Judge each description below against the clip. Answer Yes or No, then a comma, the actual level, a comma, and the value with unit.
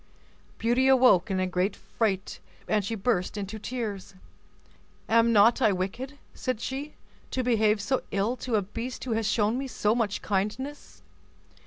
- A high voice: Yes, high, 220 Hz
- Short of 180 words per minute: Yes, average, 160 wpm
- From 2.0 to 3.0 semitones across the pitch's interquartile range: No, average, 3.8 semitones